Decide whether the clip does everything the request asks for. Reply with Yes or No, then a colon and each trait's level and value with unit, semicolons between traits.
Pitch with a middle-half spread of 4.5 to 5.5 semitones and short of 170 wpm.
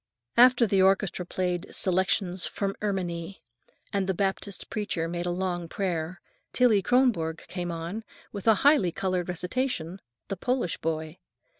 No: average, 2.7 semitones; average, 140 wpm